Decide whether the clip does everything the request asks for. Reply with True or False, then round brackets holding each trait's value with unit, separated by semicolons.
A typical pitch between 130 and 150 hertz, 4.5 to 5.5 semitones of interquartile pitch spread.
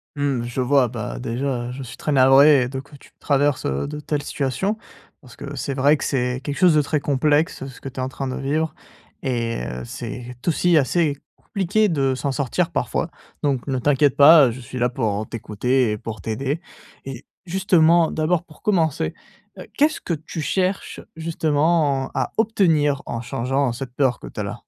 False (140 Hz; 3.6 semitones)